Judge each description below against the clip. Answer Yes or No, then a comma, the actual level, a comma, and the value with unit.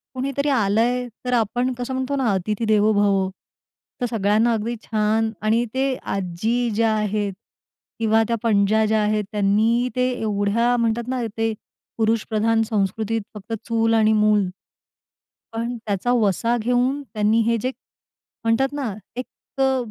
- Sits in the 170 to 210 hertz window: No, high, 225 Hz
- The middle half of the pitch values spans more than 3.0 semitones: No, narrow, 2.4 semitones